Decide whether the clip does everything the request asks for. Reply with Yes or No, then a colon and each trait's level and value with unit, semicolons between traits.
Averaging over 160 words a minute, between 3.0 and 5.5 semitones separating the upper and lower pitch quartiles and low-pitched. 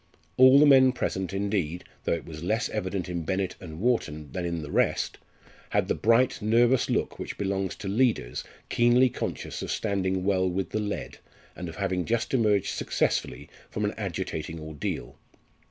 Yes: average, 170 wpm; average, 5.1 semitones; very low, 95 Hz